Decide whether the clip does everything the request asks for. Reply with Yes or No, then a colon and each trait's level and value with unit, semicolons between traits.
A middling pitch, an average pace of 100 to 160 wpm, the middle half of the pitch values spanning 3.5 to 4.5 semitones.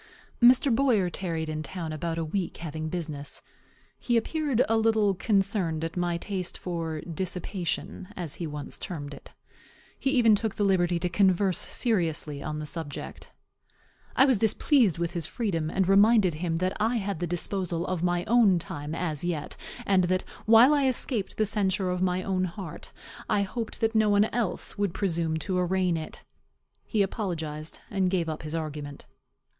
No: medium, 180 Hz; average, 170 wpm; average, 4.0 semitones